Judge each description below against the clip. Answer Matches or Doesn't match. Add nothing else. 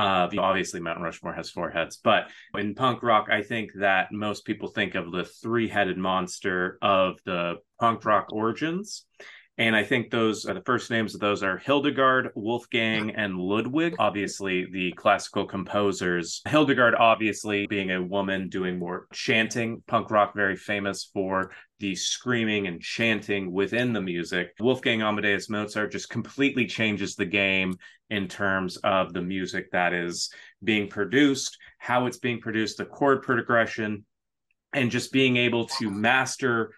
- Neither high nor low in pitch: Doesn't match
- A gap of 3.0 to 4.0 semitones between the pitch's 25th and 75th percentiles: Matches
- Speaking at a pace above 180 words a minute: Doesn't match